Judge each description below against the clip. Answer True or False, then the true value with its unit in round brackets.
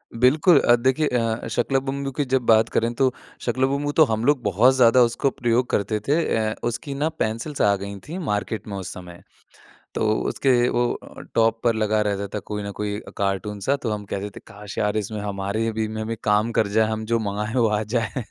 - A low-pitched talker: True (110 Hz)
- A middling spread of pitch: True (3.3 semitones)